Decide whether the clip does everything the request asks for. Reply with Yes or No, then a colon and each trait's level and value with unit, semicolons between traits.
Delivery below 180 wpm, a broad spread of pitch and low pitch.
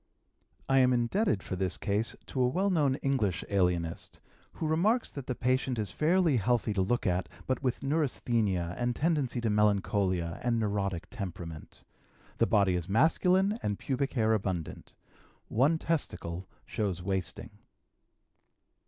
Yes: average, 145 wpm; wide, 6.2 semitones; low, 115 Hz